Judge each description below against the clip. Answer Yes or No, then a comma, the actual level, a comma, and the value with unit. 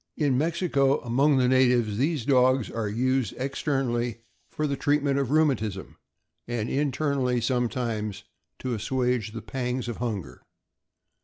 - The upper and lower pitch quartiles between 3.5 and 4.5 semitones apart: No, average, 2.8 semitones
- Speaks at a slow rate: Yes, slow, 130 wpm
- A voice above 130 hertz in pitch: No, low, 125 Hz